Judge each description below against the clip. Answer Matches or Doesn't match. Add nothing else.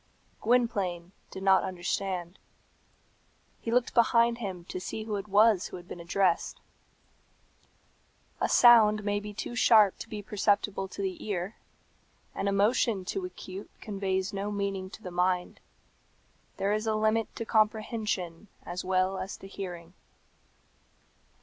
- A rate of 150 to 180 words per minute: Doesn't match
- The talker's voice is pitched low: Doesn't match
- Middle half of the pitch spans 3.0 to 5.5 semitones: Doesn't match